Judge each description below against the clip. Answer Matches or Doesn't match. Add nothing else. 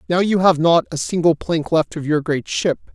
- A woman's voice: Doesn't match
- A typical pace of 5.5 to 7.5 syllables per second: Doesn't match